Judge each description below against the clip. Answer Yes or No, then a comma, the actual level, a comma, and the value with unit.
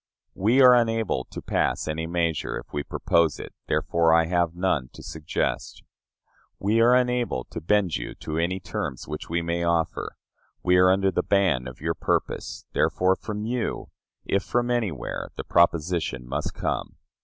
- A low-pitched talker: Yes, very low, 85 Hz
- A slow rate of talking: No, average, 165 wpm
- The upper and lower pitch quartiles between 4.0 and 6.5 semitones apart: Yes, average, 4.4 semitones